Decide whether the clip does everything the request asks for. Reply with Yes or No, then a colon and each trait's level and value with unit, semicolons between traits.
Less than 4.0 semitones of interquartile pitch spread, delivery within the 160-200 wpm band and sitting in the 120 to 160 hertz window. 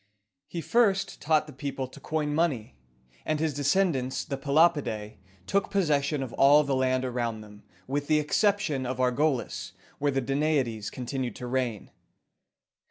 Yes: average, 3.4 semitones; average, 165 wpm; medium, 140 Hz